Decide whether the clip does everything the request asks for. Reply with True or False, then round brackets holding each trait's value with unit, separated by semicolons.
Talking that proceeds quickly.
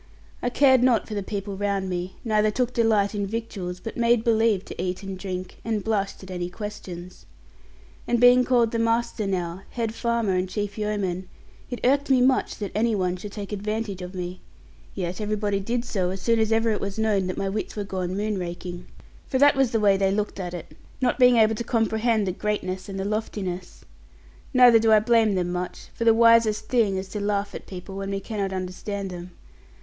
True (210 wpm)